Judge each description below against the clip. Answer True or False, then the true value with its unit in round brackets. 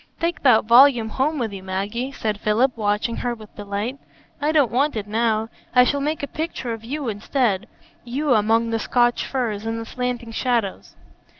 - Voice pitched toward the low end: False (235 Hz)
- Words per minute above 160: True (180 wpm)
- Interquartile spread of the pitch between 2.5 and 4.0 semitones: True (3.5 semitones)